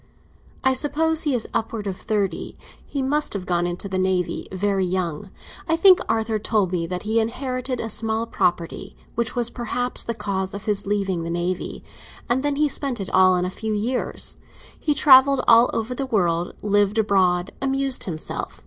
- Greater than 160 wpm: Yes, average, 175 wpm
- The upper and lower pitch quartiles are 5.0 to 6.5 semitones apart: Yes, average, 5.3 semitones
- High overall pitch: Yes, high, 215 Hz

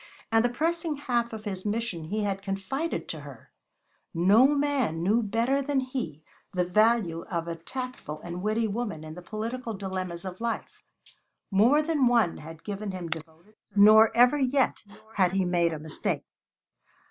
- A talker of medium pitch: No, high, 210 Hz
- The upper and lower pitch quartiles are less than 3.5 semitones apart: No, wide, 5.5 semitones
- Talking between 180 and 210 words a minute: No, average, 170 wpm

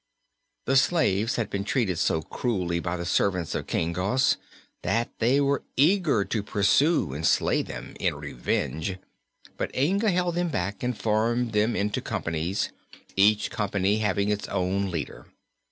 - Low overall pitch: Yes, low, 105 Hz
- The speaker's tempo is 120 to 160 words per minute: Yes, average, 155 wpm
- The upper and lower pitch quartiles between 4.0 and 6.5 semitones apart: Yes, average, 5.2 semitones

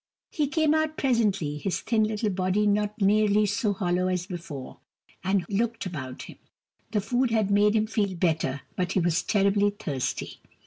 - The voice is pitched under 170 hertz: No, high, 200 Hz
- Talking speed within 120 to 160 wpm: No, average, 170 wpm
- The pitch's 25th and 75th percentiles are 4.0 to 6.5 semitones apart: No, average, 3.1 semitones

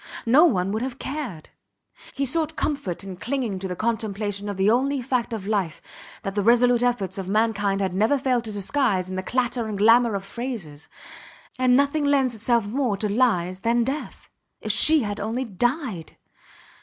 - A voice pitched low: No, high, 225 Hz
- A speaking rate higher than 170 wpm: Yes, average, 180 wpm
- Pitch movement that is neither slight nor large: Yes, average, 4.5 semitones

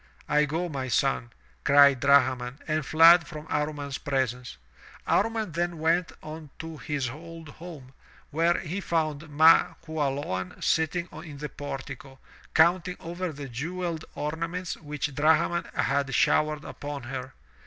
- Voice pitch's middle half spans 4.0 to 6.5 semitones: No, average, 3.0 semitones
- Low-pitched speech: No, medium, 150 Hz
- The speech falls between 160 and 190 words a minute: No, slow, 135 wpm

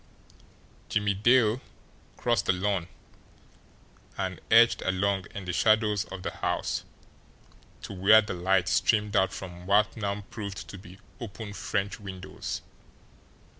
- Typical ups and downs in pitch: No, narrow, 1.9 semitones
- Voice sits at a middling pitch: No, low, 100 Hz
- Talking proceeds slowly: Yes, slow, 130 wpm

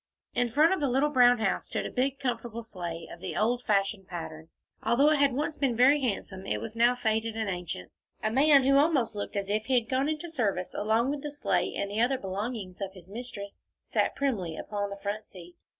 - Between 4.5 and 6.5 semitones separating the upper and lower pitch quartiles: Yes, average, 5.0 semitones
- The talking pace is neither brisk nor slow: No, fast, 225 wpm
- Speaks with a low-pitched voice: No, high, 225 Hz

